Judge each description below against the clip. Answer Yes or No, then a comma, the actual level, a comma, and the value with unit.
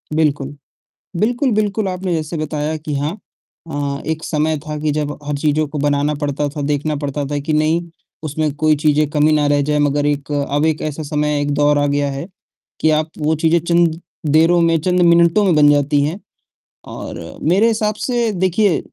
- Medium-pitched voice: Yes, medium, 155 Hz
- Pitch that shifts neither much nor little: No, narrow, 2.3 semitones